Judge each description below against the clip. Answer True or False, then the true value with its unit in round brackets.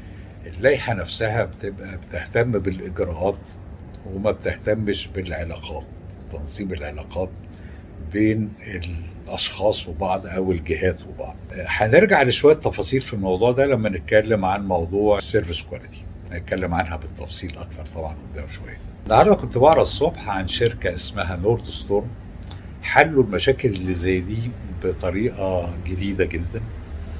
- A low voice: True (95 Hz)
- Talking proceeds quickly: False (115 wpm)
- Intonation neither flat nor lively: True (3.1 semitones)